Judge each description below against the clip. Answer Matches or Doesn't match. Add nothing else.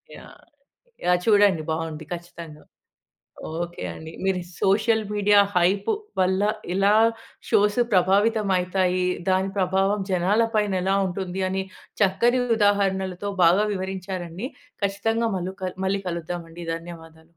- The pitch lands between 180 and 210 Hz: Matches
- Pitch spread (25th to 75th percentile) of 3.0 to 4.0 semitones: Doesn't match